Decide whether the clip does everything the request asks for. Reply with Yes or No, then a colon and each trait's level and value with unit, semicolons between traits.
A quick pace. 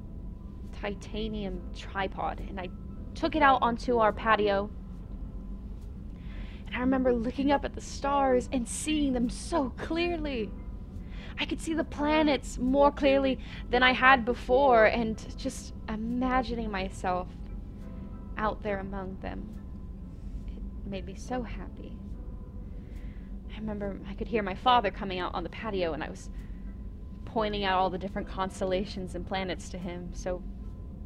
No: average, 140 wpm